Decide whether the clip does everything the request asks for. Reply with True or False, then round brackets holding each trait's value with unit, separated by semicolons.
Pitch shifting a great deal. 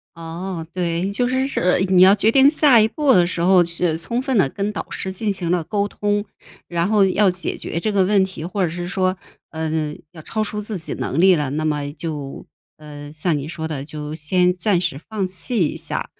False (4.2 semitones)